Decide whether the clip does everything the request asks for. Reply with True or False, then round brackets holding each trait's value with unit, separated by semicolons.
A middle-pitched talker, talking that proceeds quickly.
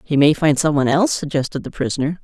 True (155 Hz; 240 wpm)